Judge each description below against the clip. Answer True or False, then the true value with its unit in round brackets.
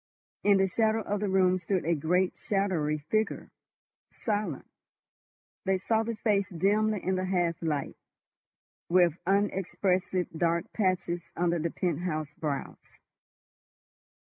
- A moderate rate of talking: False (115 wpm)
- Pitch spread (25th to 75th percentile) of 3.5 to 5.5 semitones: False (2.9 semitones)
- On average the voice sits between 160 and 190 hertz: True (185 Hz)